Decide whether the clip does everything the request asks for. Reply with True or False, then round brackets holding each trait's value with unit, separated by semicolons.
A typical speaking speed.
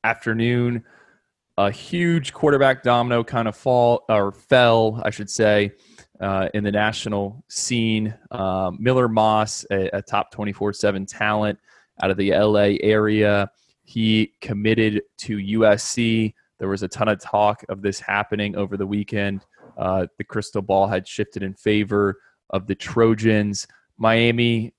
True (145 wpm)